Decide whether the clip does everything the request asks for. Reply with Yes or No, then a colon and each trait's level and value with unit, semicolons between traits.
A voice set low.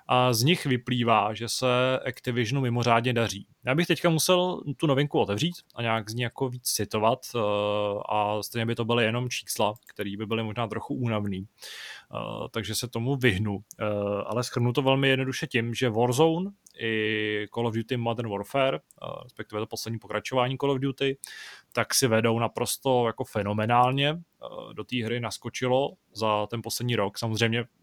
Yes: low, 120 Hz